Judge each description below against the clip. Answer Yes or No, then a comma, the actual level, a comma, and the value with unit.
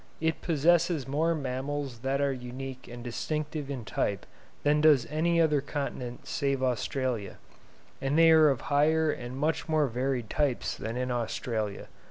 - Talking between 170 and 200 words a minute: No, average, 155 wpm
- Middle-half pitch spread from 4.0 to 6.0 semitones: No, average, 3.6 semitones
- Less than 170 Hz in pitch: Yes, medium, 140 Hz